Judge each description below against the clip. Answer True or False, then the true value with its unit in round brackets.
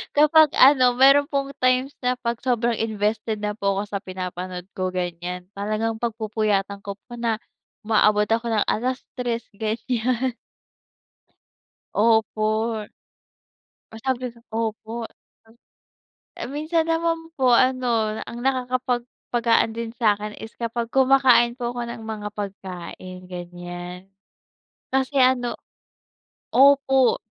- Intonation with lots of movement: False (3.5 semitones)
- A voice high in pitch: True (230 Hz)